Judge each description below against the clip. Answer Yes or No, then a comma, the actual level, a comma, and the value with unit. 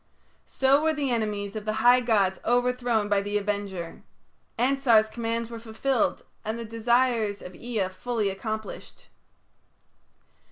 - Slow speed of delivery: Yes, slow, 130 wpm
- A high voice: Yes, high, 225 Hz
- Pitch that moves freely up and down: No, average, 3.0 semitones